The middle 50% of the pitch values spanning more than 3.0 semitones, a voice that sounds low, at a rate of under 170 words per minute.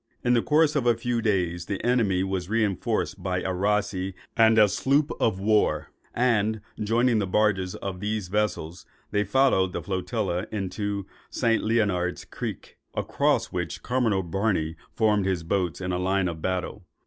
Yes: average, 3.4 semitones; low, 100 Hz; average, 160 wpm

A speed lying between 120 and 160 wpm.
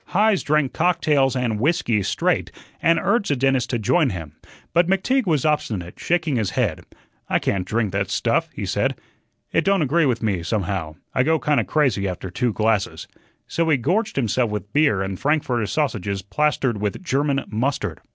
No: average, 175 wpm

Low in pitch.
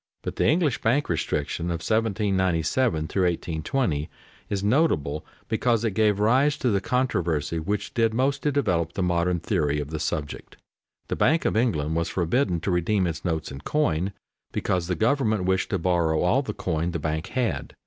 Yes: very low, 95 Hz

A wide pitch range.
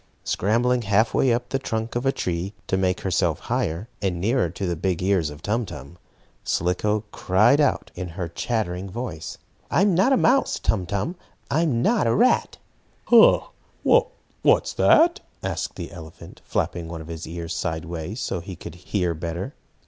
Yes: wide, 6.0 semitones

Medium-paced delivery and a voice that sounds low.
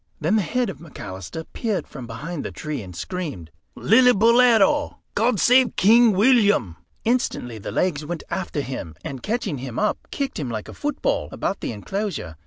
No: average, 170 wpm; medium, 185 Hz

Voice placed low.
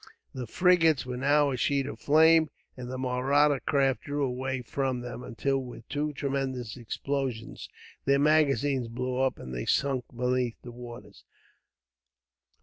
Yes: low, 130 Hz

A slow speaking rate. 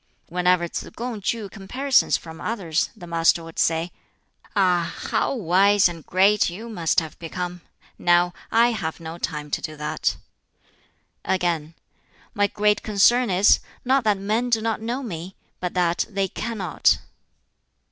No: average, 145 wpm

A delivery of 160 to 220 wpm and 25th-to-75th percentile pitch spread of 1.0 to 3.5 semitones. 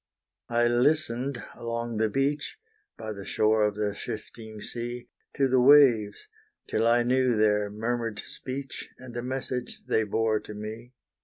No: average, 150 wpm; average, 2.8 semitones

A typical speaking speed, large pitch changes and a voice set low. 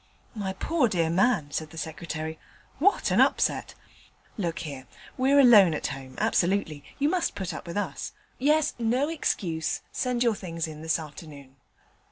No: average, 160 wpm; wide, 7.6 semitones; medium, 180 Hz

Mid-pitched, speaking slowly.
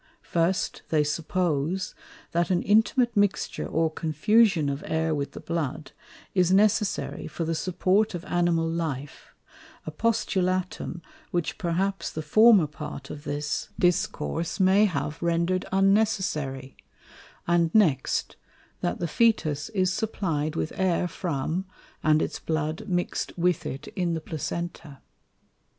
Yes: medium, 170 Hz; slow, 130 wpm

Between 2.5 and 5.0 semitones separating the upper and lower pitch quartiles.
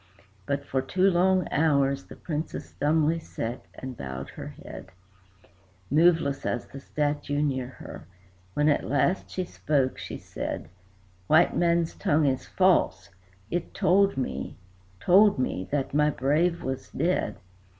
Yes: average, 4.4 semitones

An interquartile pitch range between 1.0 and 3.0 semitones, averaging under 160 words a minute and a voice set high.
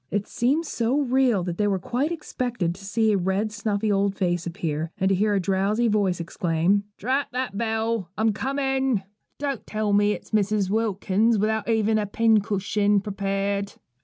No: average, 2.7 semitones; average, 170 wpm; high, 210 Hz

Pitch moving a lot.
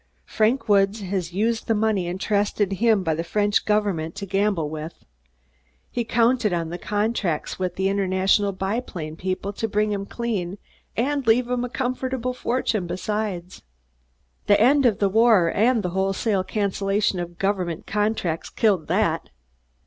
No: average, 3.3 semitones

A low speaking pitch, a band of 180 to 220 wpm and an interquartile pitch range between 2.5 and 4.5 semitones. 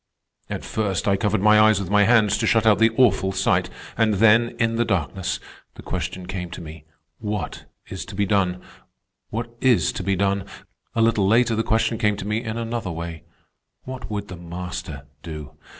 Yes: low, 105 Hz; average, 195 wpm; average, 3.4 semitones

